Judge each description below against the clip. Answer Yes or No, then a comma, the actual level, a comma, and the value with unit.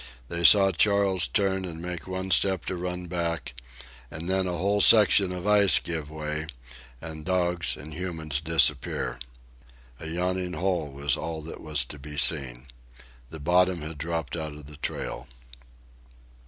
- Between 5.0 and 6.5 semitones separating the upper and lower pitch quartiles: No, average, 3.2 semitones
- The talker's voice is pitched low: Yes, very low, 85 Hz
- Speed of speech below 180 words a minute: Yes, average, 155 wpm